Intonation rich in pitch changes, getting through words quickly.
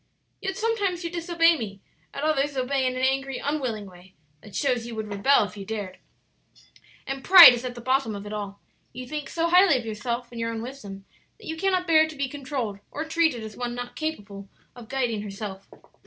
Yes: wide, 6.3 semitones; fast, 210 wpm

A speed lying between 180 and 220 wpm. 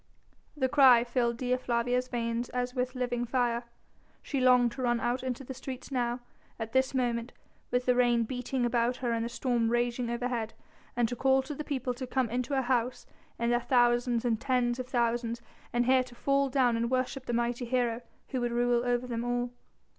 Yes: average, 200 wpm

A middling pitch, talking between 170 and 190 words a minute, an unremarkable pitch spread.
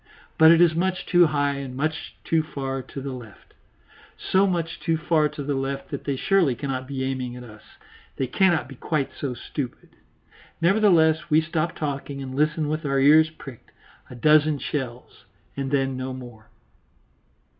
Yes: medium, 145 Hz; average, 175 wpm; average, 3.2 semitones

